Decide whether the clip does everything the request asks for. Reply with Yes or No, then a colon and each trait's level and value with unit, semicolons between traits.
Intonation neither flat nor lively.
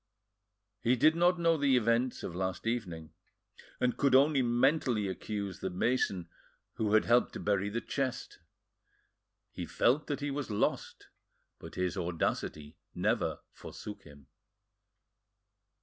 No: wide, 6.2 semitones